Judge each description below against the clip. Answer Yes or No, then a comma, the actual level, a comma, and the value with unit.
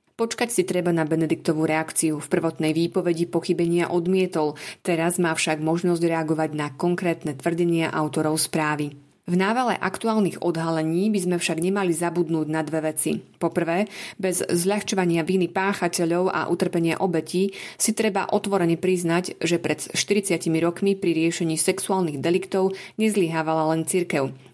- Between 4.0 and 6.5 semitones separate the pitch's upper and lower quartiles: No, narrow, 2.6 semitones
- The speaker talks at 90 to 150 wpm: Yes, average, 135 wpm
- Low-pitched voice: No, medium, 170 Hz